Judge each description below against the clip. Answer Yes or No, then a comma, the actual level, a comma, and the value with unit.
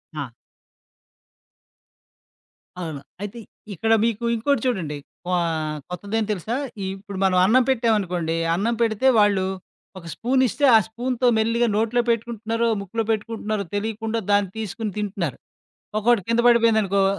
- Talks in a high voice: Yes, high, 220 Hz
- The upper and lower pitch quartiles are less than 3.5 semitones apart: Yes, average, 2.8 semitones